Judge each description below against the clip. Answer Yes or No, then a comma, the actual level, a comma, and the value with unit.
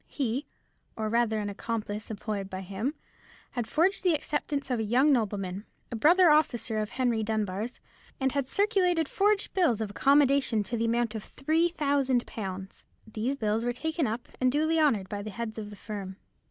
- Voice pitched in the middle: No, high, 235 Hz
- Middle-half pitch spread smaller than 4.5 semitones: No, average, 5.2 semitones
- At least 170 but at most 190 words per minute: Yes, average, 180 wpm